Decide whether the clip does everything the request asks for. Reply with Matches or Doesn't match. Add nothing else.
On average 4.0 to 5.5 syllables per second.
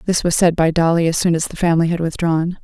Doesn't match